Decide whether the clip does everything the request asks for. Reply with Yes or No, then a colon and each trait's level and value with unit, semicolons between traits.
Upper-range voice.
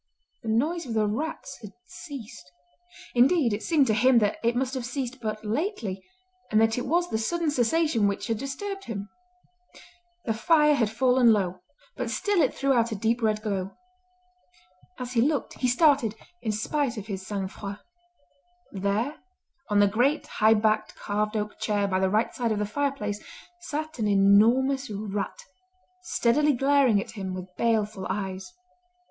Yes: high, 225 Hz